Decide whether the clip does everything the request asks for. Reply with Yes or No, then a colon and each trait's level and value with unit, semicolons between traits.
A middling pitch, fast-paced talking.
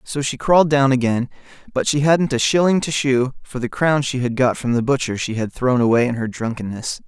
No: low, 130 Hz; fast, 240 wpm